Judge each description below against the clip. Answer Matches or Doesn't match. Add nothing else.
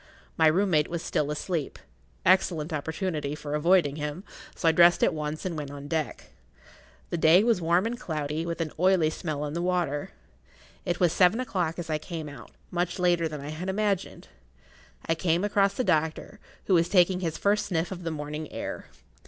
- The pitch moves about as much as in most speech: Matches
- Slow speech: Doesn't match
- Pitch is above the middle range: Doesn't match